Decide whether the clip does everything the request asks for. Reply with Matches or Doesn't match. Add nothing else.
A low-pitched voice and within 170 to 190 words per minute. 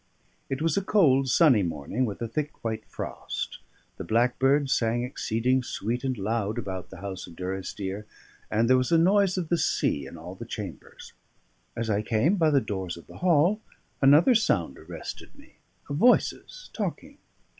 Matches